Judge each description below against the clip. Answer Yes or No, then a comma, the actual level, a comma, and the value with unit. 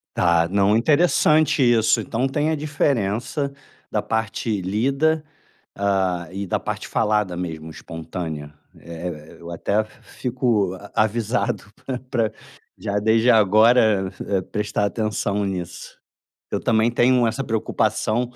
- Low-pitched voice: Yes, low, 110 Hz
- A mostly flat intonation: No, average, 4.4 semitones